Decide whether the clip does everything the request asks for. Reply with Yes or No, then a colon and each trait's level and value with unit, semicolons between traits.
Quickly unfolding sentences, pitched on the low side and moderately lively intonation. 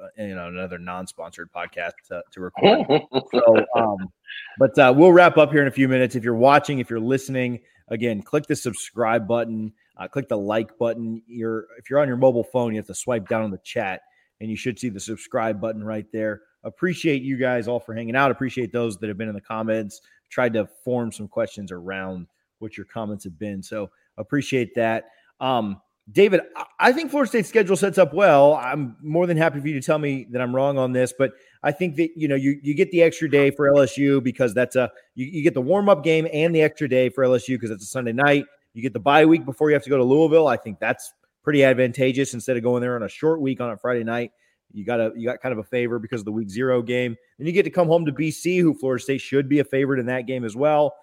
Yes: fast, 250 wpm; low, 125 Hz; average, 4.3 semitones